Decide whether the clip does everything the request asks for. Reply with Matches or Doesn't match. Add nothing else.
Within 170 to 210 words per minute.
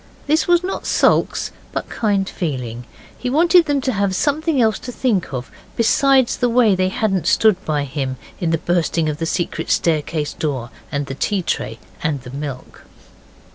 Matches